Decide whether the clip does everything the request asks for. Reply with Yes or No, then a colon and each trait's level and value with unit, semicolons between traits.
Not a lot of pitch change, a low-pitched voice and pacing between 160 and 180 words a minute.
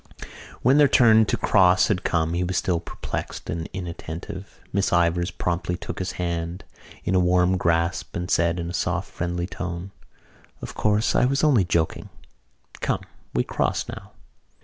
Yes: narrow, 1.9 semitones; very low, 90 Hz; average, 165 wpm